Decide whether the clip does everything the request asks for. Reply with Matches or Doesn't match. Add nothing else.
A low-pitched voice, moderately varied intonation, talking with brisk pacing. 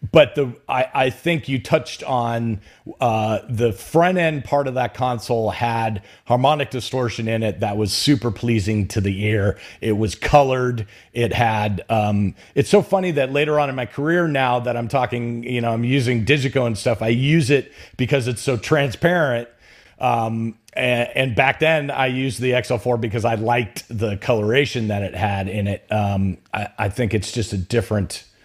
Doesn't match